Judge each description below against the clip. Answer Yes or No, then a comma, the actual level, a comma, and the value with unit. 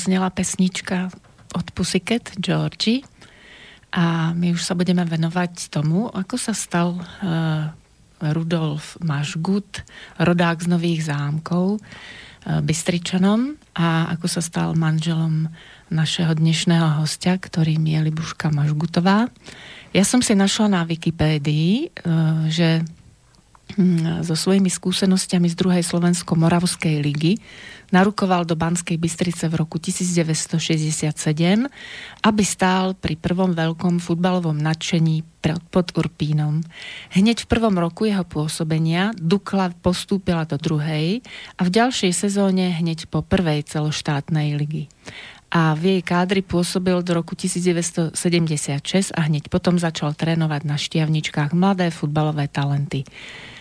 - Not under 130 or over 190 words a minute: No, average, 120 wpm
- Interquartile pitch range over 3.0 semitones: No, narrow, 2.6 semitones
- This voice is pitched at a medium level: Yes, medium, 170 Hz